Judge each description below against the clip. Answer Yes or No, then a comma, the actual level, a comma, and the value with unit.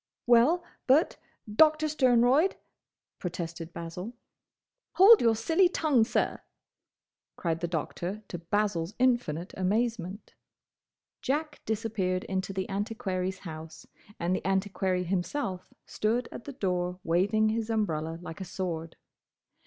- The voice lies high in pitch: Yes, high, 200 Hz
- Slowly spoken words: Yes, slow, 115 wpm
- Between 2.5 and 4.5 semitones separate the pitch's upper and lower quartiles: No, average, 5.1 semitones